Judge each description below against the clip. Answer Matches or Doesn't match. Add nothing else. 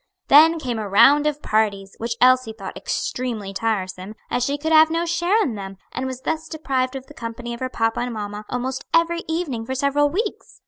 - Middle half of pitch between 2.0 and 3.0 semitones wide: Doesn't match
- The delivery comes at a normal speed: Doesn't match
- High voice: Matches